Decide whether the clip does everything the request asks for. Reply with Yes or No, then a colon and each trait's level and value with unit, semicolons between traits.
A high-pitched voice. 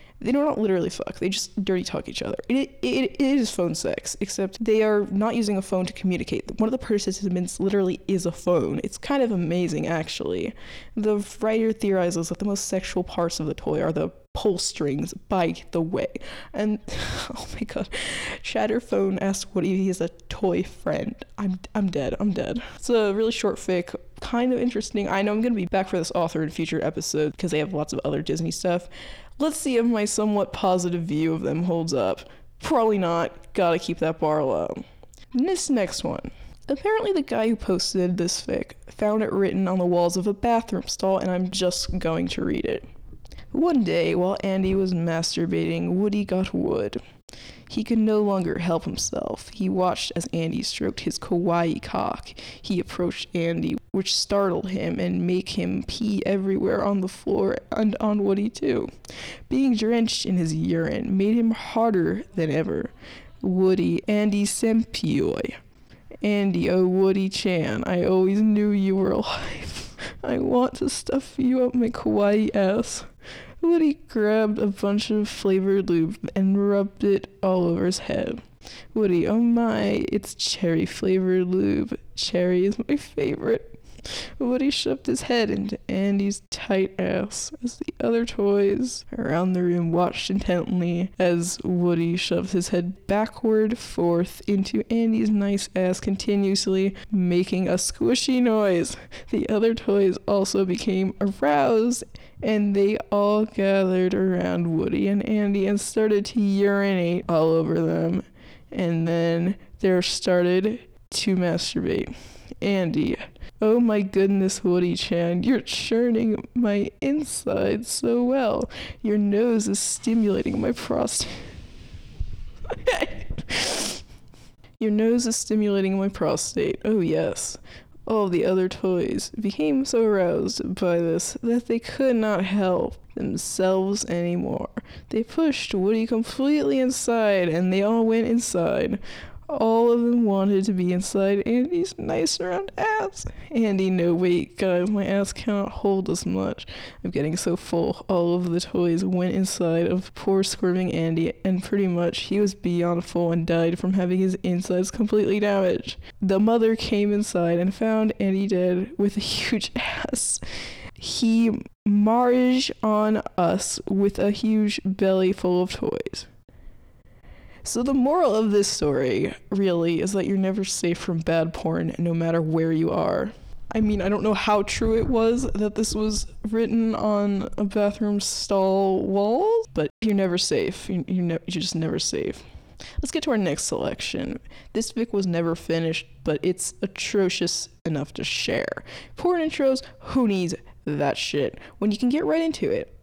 Yes: high, 200 Hz